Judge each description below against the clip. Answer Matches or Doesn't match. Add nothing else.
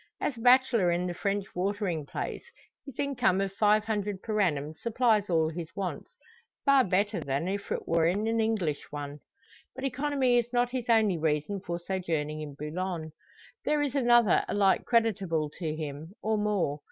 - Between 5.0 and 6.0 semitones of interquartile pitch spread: Matches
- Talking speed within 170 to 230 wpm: Matches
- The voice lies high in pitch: Matches